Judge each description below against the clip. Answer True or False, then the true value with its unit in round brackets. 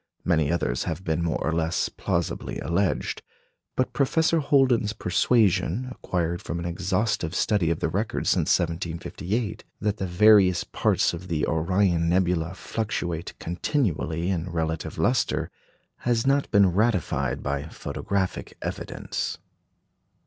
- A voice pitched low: True (90 Hz)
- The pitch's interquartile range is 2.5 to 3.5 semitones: False (4.1 semitones)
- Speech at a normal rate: False (125 wpm)